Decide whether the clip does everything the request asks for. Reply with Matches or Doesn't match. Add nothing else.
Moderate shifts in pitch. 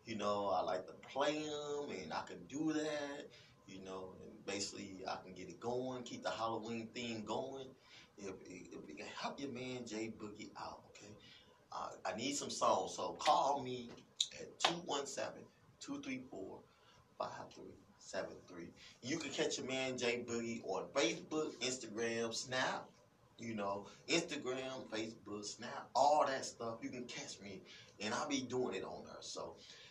Matches